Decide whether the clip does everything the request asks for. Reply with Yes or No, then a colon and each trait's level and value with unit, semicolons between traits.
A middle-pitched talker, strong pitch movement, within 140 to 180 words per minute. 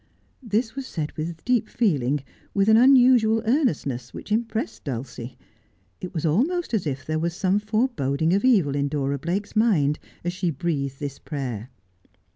Yes: medium, 170 Hz; wide, 7.8 semitones; average, 165 wpm